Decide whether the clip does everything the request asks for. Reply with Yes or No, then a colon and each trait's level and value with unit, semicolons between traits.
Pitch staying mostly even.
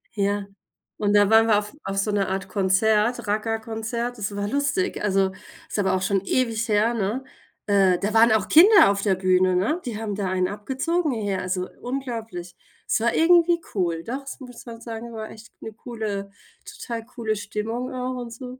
No: average, 3.3 semitones